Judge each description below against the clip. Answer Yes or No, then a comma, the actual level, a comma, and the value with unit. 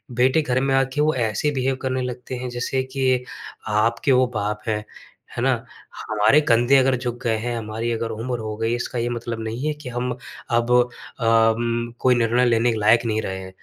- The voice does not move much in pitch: Yes, narrow, 2.1 semitones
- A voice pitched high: No, low, 120 Hz